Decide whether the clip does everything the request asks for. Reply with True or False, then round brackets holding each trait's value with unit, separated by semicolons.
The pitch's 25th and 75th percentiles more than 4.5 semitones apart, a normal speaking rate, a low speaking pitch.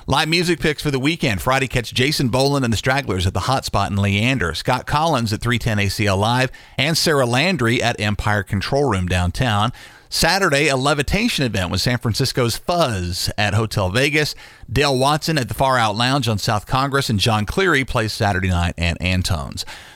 True (5.0 semitones; 185 wpm; 125 Hz)